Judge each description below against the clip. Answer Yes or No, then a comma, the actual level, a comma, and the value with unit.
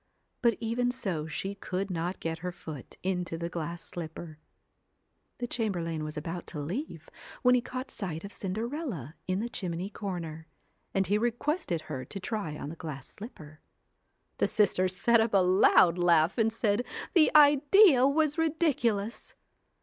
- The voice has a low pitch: No, high, 190 Hz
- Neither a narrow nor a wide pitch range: No, wide, 6.2 semitones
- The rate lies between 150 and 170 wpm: Yes, average, 155 wpm